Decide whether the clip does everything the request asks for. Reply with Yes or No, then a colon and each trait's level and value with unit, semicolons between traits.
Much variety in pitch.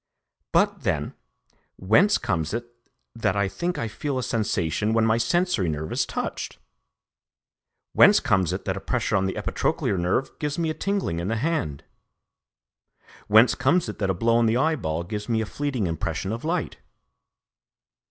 Yes: wide, 7.2 semitones